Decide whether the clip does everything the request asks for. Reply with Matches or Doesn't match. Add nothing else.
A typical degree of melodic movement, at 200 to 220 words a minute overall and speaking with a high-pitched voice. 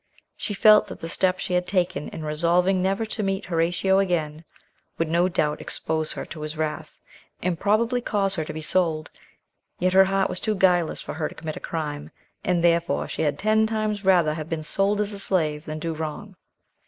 Doesn't match